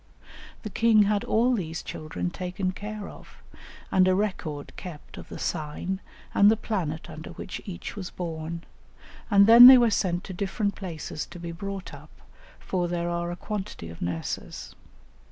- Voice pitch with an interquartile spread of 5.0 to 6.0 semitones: No, average, 3.4 semitones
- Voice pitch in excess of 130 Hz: Yes, medium, 185 Hz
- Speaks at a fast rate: No, average, 170 wpm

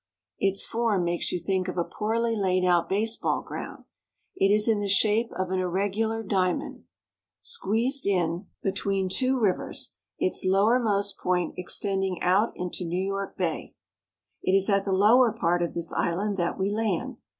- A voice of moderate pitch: No, high, 195 Hz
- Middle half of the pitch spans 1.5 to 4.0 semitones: Yes, average, 2.7 semitones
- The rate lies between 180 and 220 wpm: No, average, 170 wpm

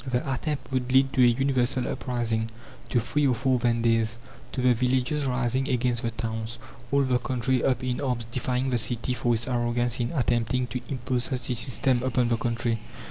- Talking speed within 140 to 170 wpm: No, average, 190 wpm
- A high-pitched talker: No, low, 125 Hz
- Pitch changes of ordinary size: No, narrow, 1.7 semitones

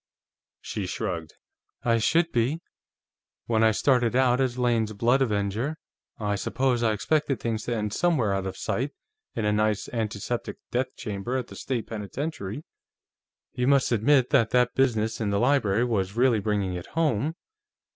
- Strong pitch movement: No, average, 3.8 semitones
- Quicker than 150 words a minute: Yes, average, 160 wpm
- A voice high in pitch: No, low, 115 Hz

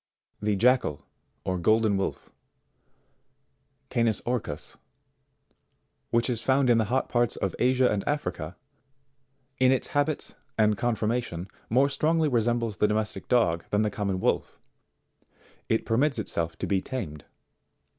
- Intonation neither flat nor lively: Yes, average, 4.1 semitones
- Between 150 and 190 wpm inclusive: No, slow, 135 wpm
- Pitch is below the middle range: Yes, low, 115 Hz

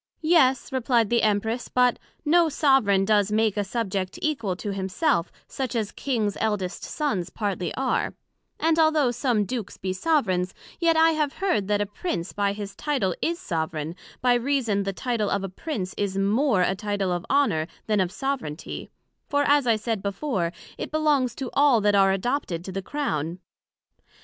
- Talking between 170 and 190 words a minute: Yes, average, 175 wpm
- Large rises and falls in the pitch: Yes, wide, 6.2 semitones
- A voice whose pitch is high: Yes, high, 215 Hz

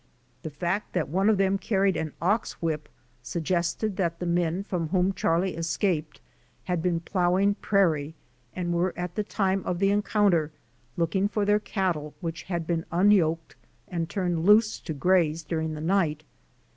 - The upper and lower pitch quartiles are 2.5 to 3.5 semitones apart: Yes, average, 3.0 semitones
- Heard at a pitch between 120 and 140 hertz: No, medium, 175 Hz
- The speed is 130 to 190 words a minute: Yes, average, 165 wpm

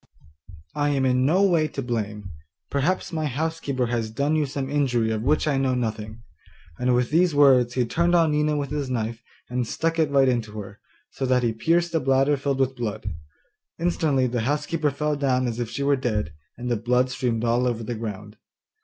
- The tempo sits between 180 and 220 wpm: Yes, fast, 205 wpm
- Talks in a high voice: No, low, 130 Hz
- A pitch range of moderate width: Yes, average, 3.8 semitones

